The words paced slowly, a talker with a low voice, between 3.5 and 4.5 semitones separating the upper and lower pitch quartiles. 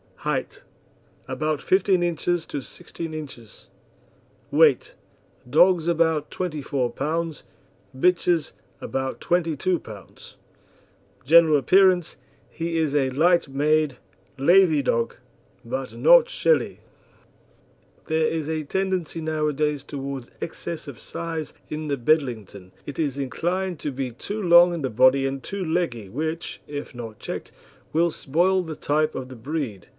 No: slow, 130 wpm; medium, 155 Hz; average, 4.0 semitones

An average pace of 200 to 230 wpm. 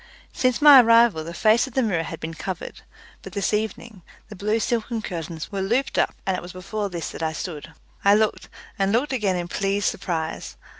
Yes: fast, 205 wpm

